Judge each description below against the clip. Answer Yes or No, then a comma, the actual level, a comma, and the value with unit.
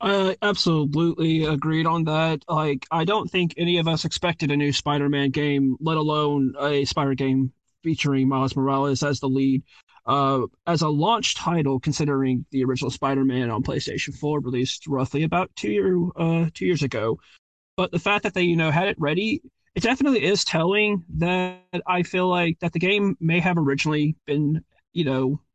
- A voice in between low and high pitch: Yes, medium, 155 Hz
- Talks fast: No, average, 180 wpm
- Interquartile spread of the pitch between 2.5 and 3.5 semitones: No, average, 4.2 semitones